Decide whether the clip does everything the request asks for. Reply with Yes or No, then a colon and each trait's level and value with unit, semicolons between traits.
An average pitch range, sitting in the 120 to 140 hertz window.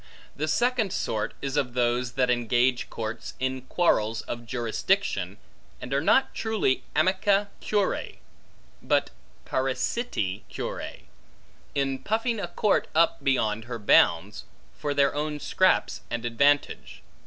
No: wide, 7.4 semitones; low, 135 Hz